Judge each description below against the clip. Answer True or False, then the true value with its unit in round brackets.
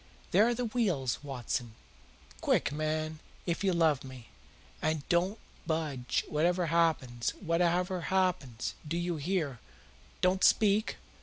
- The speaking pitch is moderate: True (165 Hz)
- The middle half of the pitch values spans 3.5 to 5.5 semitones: True (4.5 semitones)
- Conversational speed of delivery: False (125 wpm)